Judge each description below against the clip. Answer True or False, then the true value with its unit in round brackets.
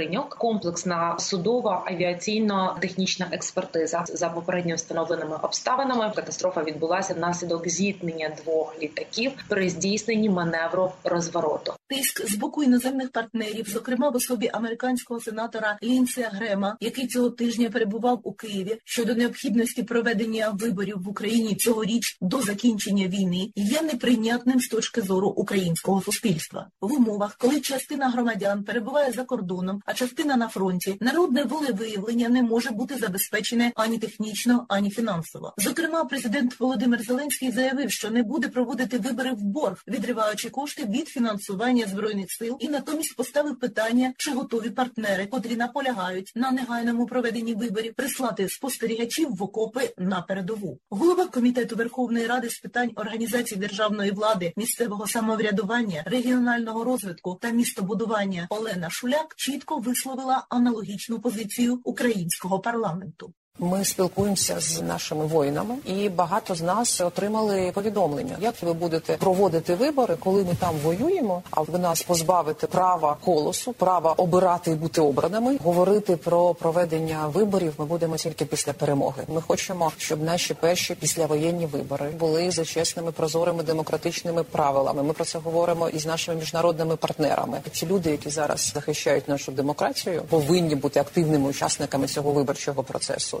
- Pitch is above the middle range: True (210 Hz)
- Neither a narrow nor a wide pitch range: False (5.7 semitones)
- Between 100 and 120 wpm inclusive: False (135 wpm)